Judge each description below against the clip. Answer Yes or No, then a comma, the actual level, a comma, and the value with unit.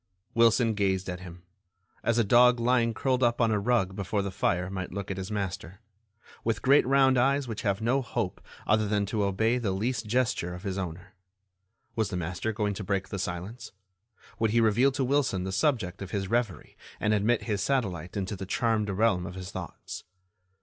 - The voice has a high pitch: No, low, 105 Hz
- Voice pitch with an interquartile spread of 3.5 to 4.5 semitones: Yes, average, 3.9 semitones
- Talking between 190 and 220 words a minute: Yes, average, 200 wpm